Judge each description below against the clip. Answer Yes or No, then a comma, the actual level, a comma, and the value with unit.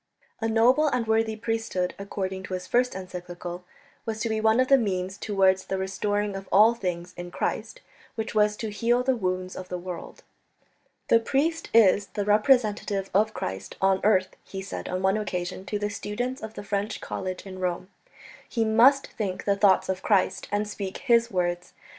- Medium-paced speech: Yes, average, 185 wpm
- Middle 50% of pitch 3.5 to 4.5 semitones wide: No, average, 3.1 semitones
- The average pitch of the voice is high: Yes, high, 205 Hz